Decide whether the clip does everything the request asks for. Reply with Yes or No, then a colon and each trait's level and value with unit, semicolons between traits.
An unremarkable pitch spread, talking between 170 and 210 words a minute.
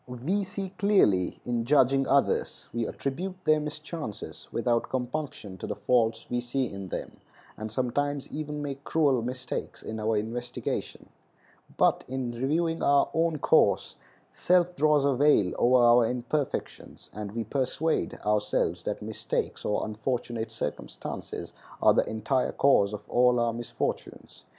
No: average, 4.4 semitones; average, 140 wpm